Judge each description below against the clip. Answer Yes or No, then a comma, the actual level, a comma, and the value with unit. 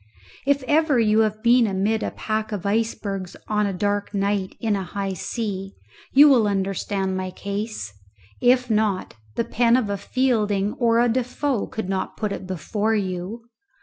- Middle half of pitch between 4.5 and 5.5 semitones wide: No, average, 2.9 semitones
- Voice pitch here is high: Yes, high, 210 Hz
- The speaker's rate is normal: Yes, average, 170 wpm